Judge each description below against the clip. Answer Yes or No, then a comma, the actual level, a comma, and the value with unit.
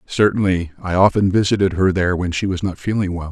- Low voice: Yes, very low, 95 Hz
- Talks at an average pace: No, fast, 215 wpm